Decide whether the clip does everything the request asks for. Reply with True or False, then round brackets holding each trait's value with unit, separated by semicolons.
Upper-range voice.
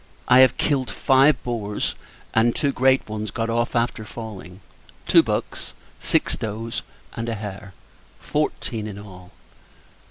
False (115 Hz)